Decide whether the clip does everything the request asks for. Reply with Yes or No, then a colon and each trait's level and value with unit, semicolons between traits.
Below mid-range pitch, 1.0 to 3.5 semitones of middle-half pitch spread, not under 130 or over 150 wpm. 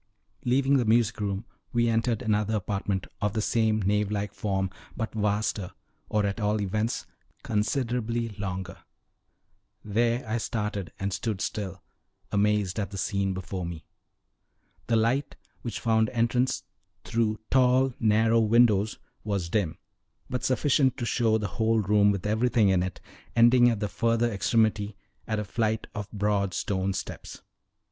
Yes: low, 105 Hz; narrow, 2.5 semitones; average, 145 wpm